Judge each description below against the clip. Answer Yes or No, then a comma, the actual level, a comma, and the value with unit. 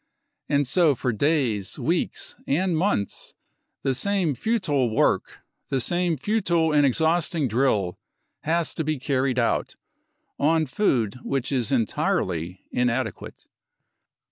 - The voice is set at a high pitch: No, medium, 140 Hz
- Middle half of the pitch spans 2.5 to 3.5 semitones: No, average, 5.0 semitones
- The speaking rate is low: Yes, slow, 115 wpm